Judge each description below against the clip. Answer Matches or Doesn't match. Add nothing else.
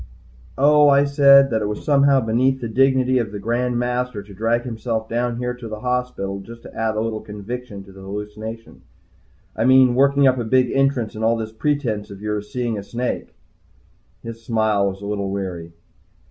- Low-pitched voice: Matches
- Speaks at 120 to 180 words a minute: Doesn't match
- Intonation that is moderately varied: Matches